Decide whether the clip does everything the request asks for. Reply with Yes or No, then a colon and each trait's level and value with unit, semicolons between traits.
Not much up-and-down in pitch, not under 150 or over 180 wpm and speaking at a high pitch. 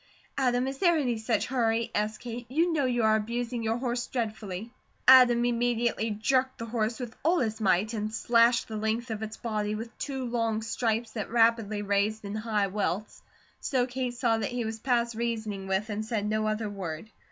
No: narrow, 2.1 semitones; average, 195 wpm; high, 225 Hz